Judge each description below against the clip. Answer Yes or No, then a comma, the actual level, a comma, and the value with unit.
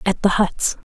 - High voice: Yes, high, 195 Hz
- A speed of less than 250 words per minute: Yes, average, 200 wpm